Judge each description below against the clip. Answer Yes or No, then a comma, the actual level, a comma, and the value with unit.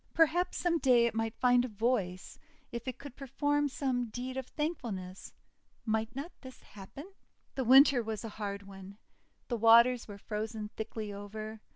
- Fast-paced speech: No, average, 165 wpm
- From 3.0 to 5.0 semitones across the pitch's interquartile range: Yes, average, 3.7 semitones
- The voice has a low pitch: No, high, 235 Hz